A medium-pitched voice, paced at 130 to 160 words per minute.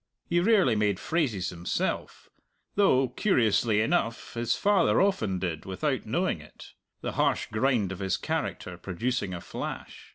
No: low, 110 Hz; average, 140 wpm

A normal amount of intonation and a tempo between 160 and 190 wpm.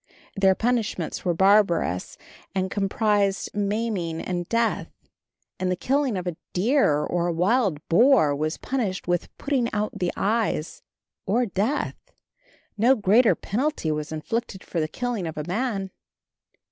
No: average, 4.9 semitones; average, 140 wpm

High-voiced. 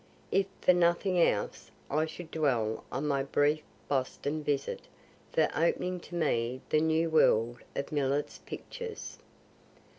No: medium, 155 Hz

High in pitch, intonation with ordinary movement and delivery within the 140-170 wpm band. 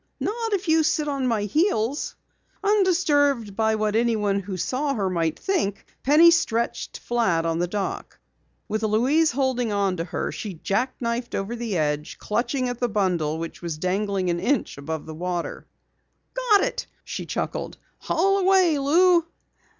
No: high, 235 Hz; wide, 8.0 semitones; average, 155 wpm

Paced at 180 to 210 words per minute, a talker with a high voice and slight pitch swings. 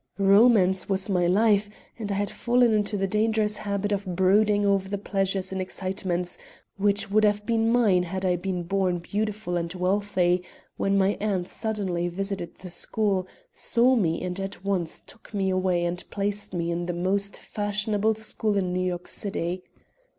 No: average, 170 wpm; high, 195 Hz; narrow, 2.3 semitones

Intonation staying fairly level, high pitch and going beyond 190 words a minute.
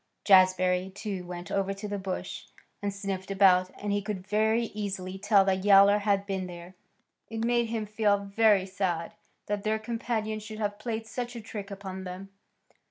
No: narrow, 2.2 semitones; high, 200 Hz; average, 175 wpm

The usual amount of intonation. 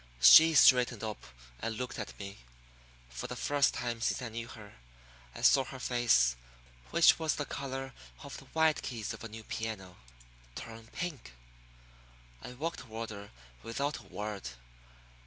Yes: average, 4.0 semitones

